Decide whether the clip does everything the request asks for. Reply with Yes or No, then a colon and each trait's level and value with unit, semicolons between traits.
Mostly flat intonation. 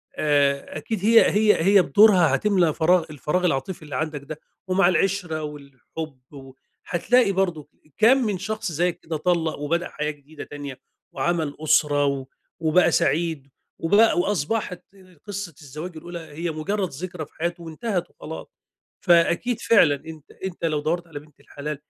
No: average, 3.7 semitones